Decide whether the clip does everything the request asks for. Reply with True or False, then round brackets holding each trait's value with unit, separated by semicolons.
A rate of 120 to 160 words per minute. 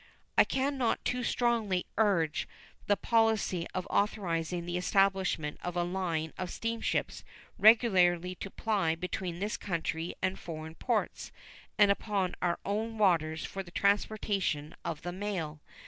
True (140 wpm)